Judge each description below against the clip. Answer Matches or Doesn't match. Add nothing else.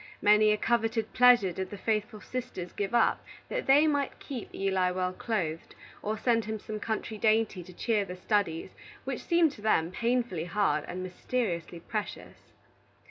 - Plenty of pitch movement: Doesn't match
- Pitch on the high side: Matches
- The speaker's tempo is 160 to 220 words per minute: Matches